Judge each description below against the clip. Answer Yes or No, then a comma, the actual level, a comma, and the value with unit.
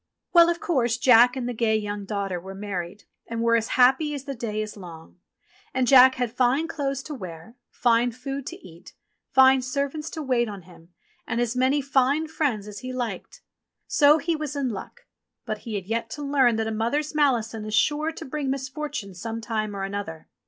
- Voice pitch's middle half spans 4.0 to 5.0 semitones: Yes, average, 4.6 semitones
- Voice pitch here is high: Yes, high, 245 Hz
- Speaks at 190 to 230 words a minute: Yes, average, 200 wpm